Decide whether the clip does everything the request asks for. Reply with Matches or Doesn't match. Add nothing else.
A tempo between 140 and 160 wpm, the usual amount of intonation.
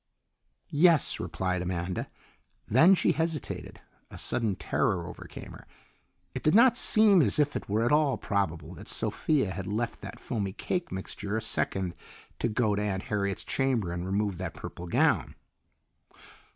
Doesn't match